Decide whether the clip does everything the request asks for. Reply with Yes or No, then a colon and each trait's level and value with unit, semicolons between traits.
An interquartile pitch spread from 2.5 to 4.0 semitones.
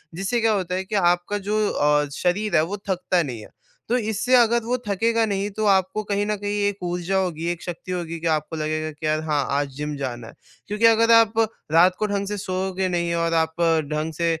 No: average, 4.4 semitones